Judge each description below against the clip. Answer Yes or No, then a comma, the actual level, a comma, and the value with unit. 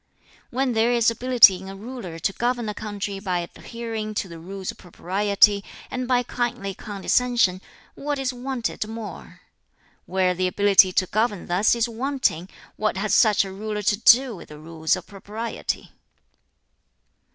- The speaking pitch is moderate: No, high, 210 Hz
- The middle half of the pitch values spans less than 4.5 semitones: Yes, average, 3.9 semitones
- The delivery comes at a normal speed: Yes, average, 160 wpm